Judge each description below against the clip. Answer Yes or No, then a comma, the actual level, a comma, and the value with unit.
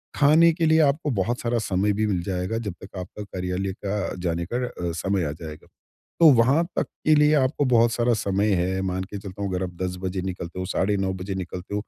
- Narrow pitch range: No, average, 4.4 semitones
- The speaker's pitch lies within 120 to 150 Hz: No, very low, 95 Hz